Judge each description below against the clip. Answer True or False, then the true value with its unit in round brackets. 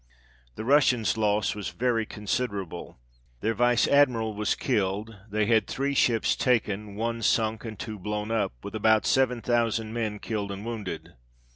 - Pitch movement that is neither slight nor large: False (2.1 semitones)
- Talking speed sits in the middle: True (150 wpm)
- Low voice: True (110 Hz)